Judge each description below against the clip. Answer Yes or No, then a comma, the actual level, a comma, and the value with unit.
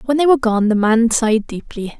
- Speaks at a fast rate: Yes, fast, 240 wpm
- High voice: Yes, high, 235 Hz